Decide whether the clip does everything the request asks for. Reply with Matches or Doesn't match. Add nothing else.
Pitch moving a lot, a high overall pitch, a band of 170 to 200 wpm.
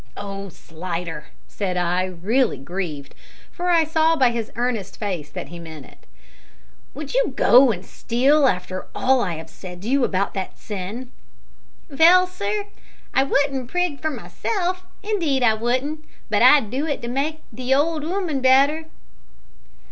Doesn't match